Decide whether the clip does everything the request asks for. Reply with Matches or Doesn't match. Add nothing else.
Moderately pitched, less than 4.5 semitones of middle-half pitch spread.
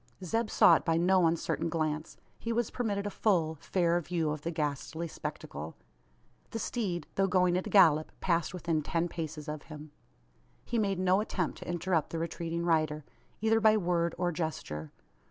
Matches